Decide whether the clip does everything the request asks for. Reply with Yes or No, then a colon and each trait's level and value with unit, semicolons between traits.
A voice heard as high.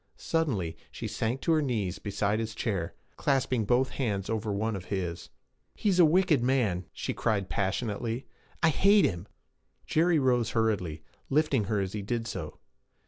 No: low, 110 Hz